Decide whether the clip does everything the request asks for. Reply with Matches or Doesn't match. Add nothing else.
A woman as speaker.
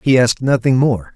Doesn't match